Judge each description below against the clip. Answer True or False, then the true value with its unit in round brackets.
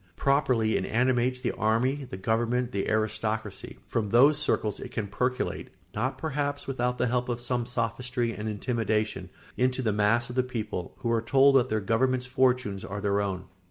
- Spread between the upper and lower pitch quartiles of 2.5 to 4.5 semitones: True (2.8 semitones)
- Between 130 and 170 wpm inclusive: False (180 wpm)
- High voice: False (120 Hz)